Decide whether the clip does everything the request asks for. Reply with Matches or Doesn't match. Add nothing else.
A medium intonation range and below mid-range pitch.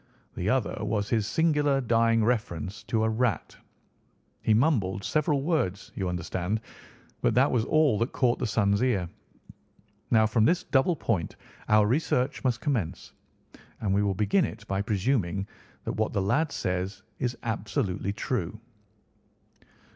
Matches